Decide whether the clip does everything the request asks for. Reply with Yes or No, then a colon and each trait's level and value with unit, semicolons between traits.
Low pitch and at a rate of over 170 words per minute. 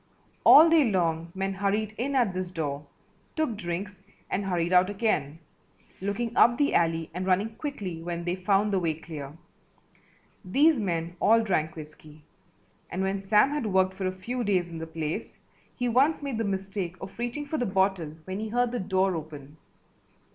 No: high, 190 Hz; average, 180 wpm